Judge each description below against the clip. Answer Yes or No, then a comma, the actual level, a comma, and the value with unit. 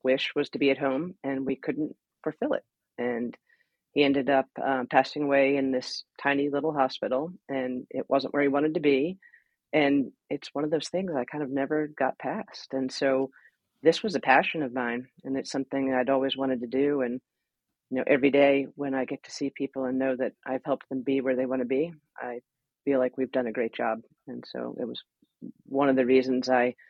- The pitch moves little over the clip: Yes, narrow, 1.5 semitones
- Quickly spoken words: Yes, fast, 220 wpm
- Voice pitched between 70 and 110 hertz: No, low, 135 Hz